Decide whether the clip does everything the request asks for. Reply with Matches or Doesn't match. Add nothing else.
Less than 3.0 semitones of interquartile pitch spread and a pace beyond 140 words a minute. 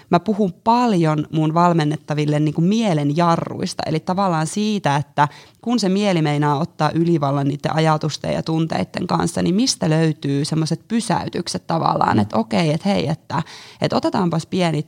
Doesn't match